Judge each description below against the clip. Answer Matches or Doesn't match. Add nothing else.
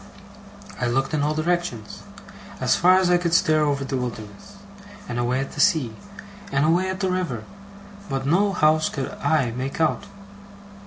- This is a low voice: Doesn't match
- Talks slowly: Doesn't match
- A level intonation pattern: Doesn't match